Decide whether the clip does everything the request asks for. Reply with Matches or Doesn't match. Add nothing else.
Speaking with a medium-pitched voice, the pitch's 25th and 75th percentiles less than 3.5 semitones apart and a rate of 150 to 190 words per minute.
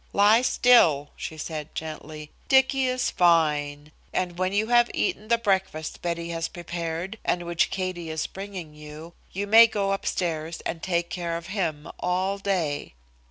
Doesn't match